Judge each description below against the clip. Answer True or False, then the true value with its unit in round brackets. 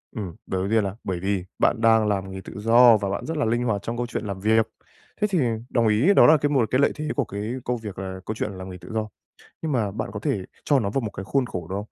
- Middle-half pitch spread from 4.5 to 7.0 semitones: False (3.9 semitones)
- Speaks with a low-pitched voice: True (110 Hz)